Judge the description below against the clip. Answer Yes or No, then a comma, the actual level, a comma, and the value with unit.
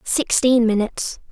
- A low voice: No, high, 235 Hz